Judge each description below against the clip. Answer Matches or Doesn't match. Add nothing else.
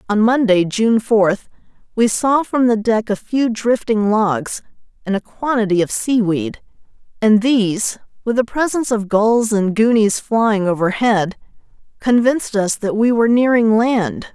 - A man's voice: Doesn't match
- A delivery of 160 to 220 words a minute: Doesn't match